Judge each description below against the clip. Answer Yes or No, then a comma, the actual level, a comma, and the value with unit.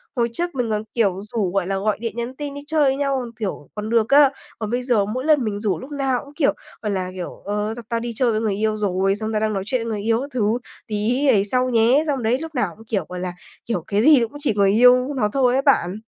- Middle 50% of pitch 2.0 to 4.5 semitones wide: Yes, average, 3.8 semitones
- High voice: Yes, high, 230 Hz